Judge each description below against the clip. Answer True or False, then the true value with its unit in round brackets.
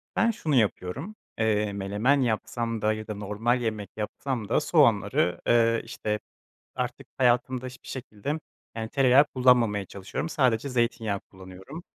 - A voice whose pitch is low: True (115 Hz)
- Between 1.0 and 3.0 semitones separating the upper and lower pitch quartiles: False (3.6 semitones)